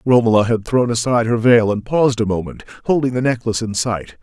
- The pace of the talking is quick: Yes, fast, 215 wpm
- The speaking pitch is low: Yes, low, 115 Hz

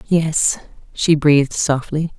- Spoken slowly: Yes, slow, 110 wpm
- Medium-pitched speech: Yes, medium, 155 Hz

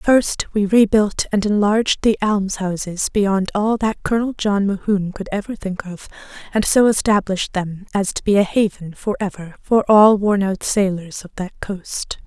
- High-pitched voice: Yes, high, 200 Hz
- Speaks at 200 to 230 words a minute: No, average, 175 wpm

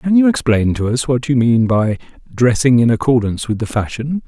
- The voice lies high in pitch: No, low, 125 Hz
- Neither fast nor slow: No, fast, 210 wpm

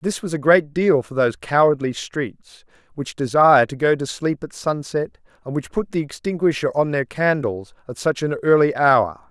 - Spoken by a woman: No, male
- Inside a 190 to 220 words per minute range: Yes, average, 195 wpm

